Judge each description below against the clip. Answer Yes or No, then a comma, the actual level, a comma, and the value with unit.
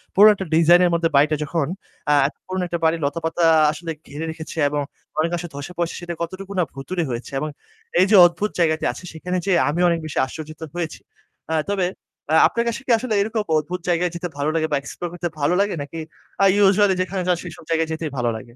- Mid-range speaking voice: Yes, medium, 170 Hz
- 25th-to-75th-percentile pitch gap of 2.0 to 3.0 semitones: Yes, narrow, 2.6 semitones